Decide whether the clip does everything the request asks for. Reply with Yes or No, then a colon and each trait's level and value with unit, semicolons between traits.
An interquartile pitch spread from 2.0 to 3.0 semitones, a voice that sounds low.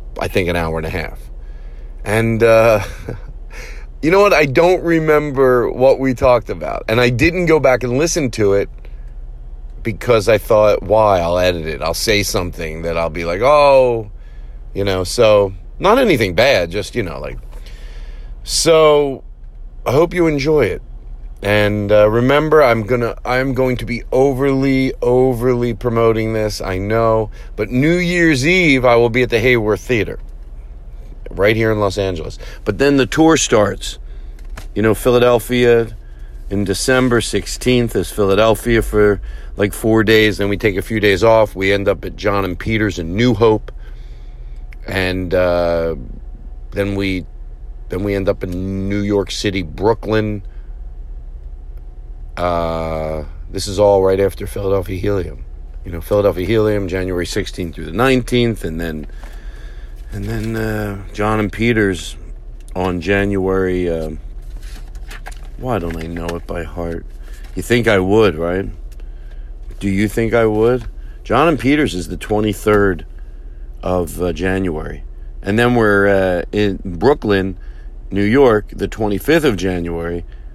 No: wide, 5.4 semitones; low, 100 Hz